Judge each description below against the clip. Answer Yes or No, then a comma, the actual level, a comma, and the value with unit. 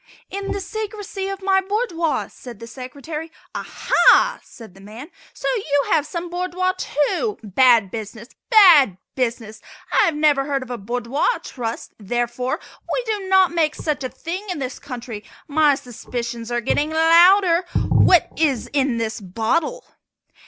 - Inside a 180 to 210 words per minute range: No, average, 150 wpm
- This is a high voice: Yes, very high, 290 Hz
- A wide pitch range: Yes, wide, 7.1 semitones